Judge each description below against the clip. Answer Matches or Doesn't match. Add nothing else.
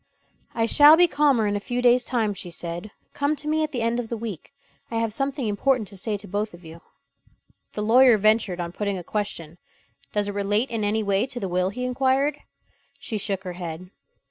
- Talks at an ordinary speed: Doesn't match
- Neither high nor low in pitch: Doesn't match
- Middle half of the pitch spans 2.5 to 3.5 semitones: Doesn't match